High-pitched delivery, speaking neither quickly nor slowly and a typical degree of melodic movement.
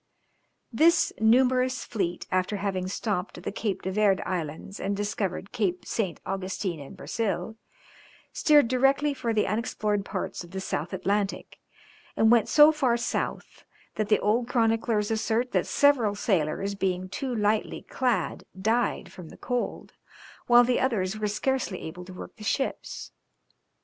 Yes: high, 210 Hz; average, 150 wpm; average, 4.3 semitones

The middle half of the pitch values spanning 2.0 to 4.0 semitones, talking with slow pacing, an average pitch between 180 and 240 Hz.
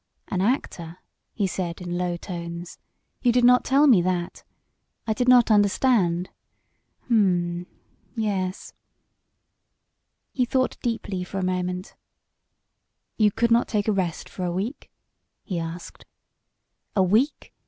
No: average, 4.7 semitones; slow, 130 wpm; high, 190 Hz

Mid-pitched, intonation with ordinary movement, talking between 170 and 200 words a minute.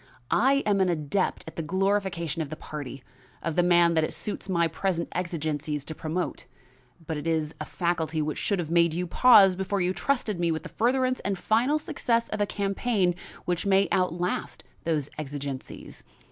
Yes: medium, 175 Hz; average, 3.8 semitones; average, 185 wpm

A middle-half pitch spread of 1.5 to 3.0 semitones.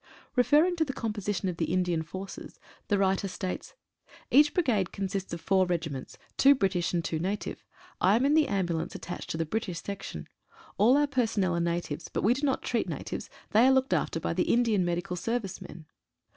No: wide, 5.6 semitones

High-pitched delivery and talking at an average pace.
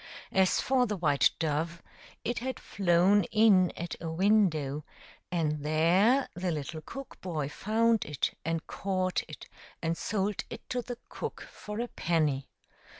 No: medium, 180 Hz; average, 150 wpm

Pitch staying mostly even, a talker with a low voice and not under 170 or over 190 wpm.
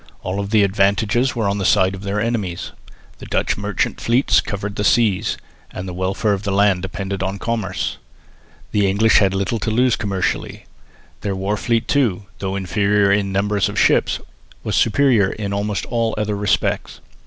Yes: narrow, 1.9 semitones; low, 100 Hz; average, 175 wpm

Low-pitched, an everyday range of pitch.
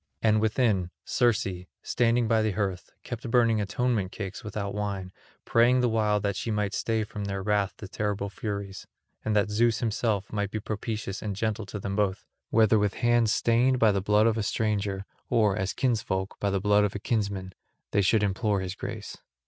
No: low, 105 Hz; narrow, 2.0 semitones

